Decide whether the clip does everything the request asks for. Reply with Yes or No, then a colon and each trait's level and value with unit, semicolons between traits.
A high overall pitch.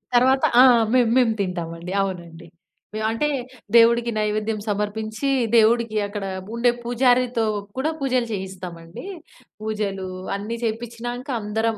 Yes: high, 220 Hz